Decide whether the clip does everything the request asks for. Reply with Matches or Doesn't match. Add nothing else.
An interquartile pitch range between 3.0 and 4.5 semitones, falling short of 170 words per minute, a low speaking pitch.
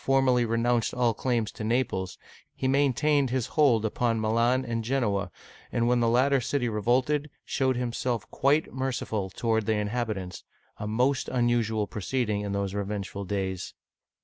Matches